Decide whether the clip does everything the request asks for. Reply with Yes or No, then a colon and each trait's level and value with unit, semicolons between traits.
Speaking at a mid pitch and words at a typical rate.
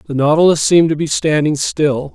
Yes: medium, 150 Hz; average, 195 wpm